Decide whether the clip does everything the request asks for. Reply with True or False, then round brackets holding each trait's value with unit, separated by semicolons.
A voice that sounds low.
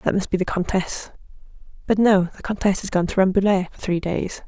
False (190 Hz)